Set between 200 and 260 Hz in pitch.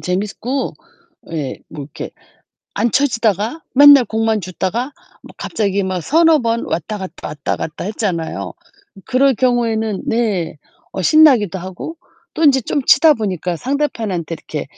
Yes: high, 220 Hz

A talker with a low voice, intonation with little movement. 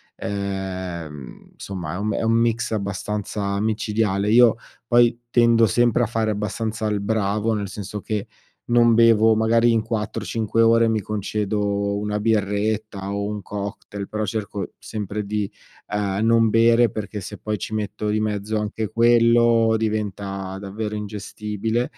Yes: low, 105 Hz; narrow, 1.9 semitones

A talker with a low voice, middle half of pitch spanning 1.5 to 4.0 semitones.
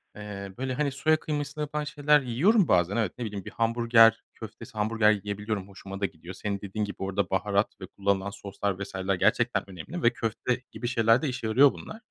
No: low, 110 Hz; average, 4.5 semitones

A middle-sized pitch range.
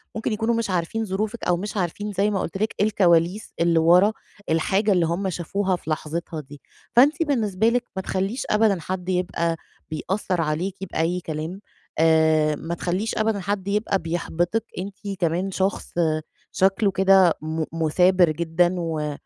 Yes: average, 3.6 semitones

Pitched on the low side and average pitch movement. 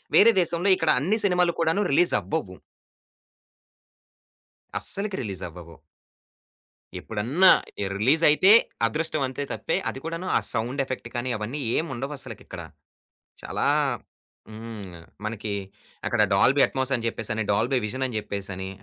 No: low, 130 Hz; wide, 7.1 semitones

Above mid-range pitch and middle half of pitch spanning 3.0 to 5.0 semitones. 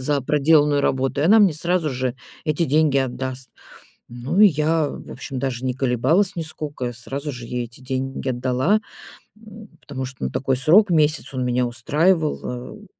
No: medium, 140 Hz; average, 3.7 semitones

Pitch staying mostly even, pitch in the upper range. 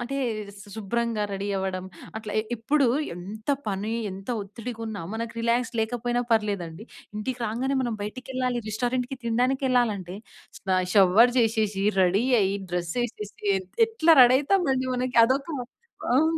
No: average, 3.7 semitones; high, 230 Hz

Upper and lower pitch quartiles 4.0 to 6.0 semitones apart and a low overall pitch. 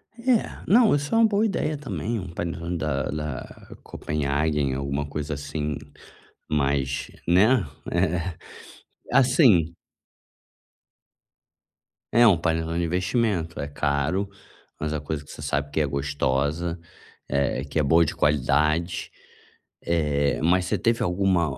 Yes: average, 4.4 semitones; very low, 80 Hz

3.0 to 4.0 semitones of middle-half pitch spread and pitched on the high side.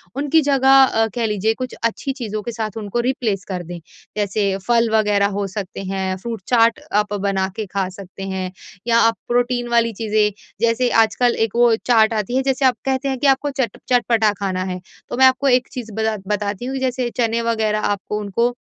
Yes: average, 3.3 semitones; high, 225 Hz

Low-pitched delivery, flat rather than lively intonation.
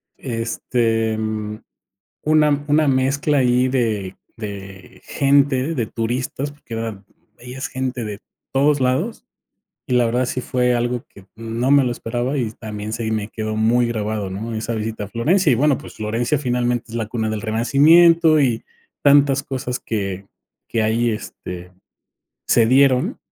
No: low, 120 Hz; average, 3.3 semitones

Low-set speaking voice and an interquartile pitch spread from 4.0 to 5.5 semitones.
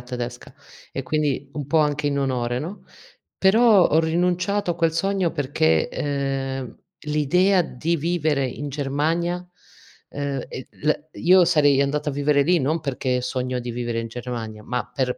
No: medium, 145 Hz; average, 4.6 semitones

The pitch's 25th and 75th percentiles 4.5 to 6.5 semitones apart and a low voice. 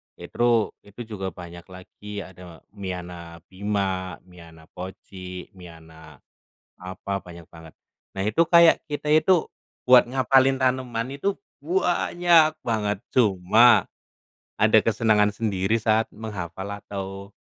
Yes: average, 5.0 semitones; low, 100 Hz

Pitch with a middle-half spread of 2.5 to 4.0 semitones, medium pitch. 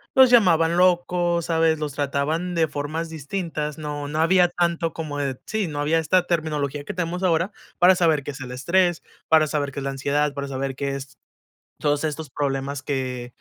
Yes: average, 3.2 semitones; medium, 155 Hz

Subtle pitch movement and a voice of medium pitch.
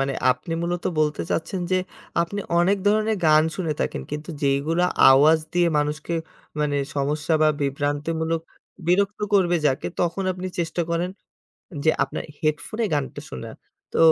No: average, 3.1 semitones; medium, 160 Hz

